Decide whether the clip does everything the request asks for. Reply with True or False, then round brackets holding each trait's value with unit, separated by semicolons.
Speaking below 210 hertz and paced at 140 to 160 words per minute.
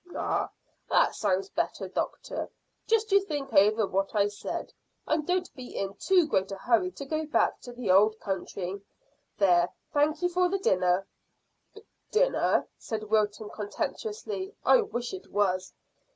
False (225 Hz; 150 wpm)